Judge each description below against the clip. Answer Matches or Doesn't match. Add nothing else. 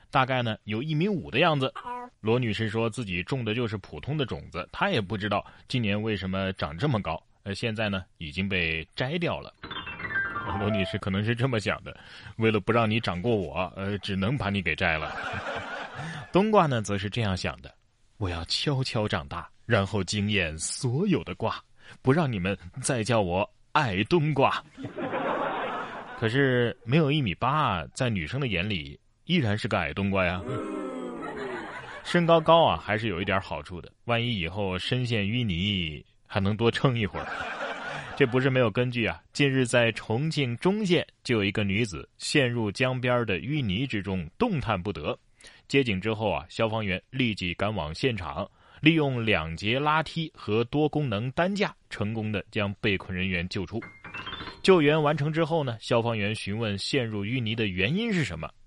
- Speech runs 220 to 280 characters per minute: Matches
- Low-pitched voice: Matches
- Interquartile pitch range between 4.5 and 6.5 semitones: Matches